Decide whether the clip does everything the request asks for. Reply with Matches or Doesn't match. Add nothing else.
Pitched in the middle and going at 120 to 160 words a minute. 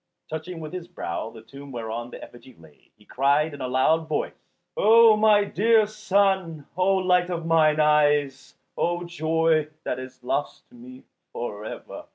Doesn't match